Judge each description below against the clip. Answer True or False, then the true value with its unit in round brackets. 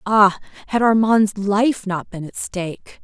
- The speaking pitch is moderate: False (205 Hz)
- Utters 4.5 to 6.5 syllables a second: False (3.9 syllables/s)